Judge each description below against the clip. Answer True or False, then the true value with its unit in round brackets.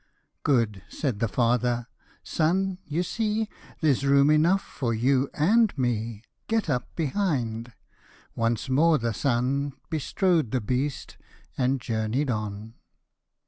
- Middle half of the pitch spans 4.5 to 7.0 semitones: True (5.1 semitones)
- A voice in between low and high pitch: False (130 Hz)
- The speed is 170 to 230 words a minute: False (135 wpm)